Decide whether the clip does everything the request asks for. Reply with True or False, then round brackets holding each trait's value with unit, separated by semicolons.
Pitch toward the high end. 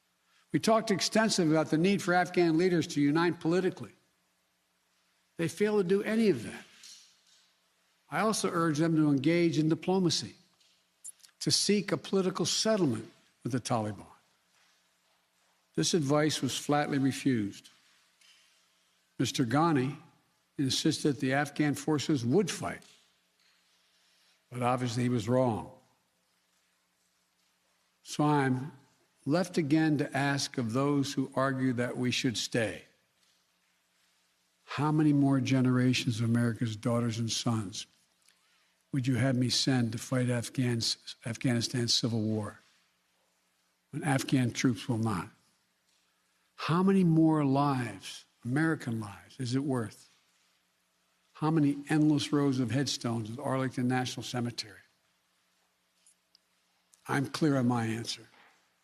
False (135 Hz)